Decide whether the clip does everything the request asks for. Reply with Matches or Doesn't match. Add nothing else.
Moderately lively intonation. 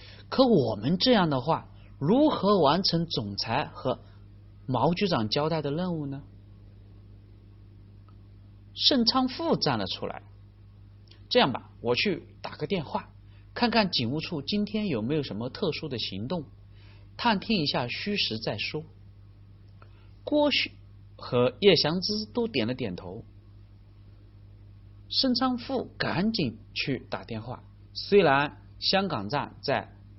Doesn't match